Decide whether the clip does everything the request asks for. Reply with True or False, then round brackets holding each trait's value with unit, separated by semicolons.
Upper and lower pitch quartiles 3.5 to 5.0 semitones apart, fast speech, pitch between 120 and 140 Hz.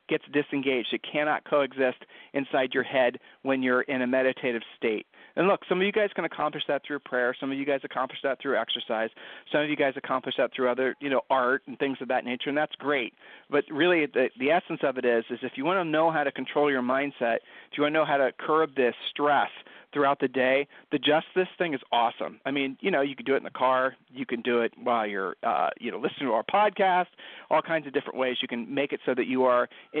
False (2.7 semitones; 255 wpm; 135 Hz)